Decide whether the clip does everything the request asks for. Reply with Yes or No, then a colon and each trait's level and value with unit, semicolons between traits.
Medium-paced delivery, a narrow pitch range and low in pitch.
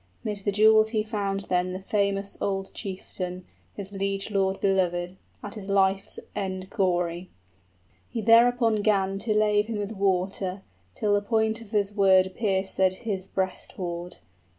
No: average, 150 wpm; narrow, 2.0 semitones; high, 195 Hz